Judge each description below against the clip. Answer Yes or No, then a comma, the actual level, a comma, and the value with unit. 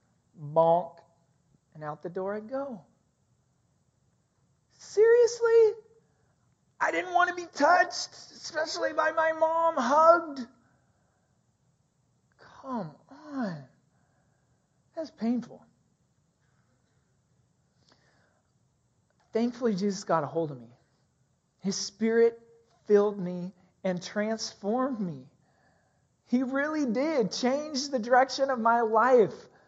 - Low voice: No, high, 220 Hz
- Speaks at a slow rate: Yes, slow, 95 wpm